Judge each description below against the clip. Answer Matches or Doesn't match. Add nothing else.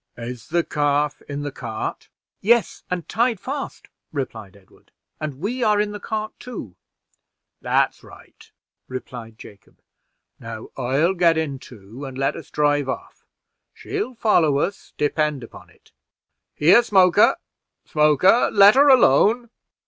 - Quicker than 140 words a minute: Doesn't match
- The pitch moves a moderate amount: Doesn't match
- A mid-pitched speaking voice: Matches